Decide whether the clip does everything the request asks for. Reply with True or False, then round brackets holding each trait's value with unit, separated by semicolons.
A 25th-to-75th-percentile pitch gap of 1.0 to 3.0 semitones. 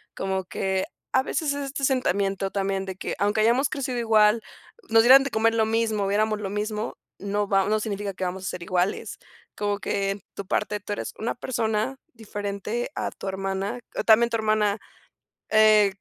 True (2.4 semitones)